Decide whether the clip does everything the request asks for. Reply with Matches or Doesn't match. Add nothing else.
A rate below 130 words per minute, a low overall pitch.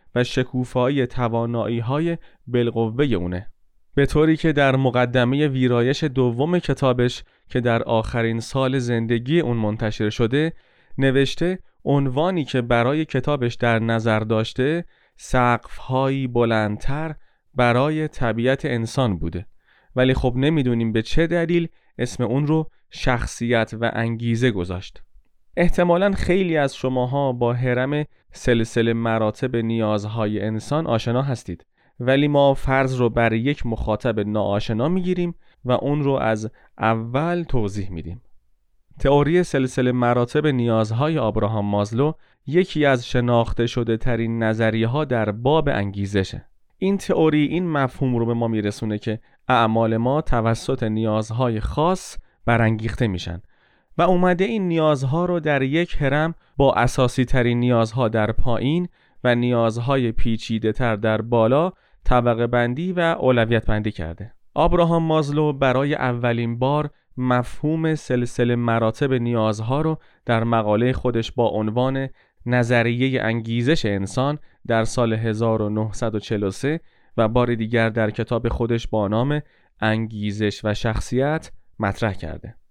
Matches